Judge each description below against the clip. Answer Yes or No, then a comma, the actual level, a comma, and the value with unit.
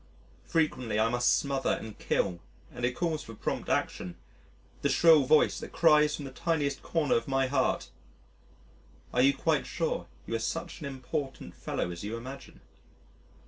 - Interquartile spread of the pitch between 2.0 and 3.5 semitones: No, average, 4.2 semitones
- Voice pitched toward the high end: No, low, 135 Hz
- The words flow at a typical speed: Yes, average, 165 wpm